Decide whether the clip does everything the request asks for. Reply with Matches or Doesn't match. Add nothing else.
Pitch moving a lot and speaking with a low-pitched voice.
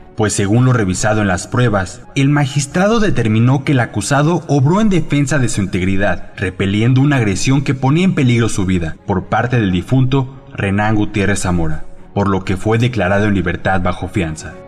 Matches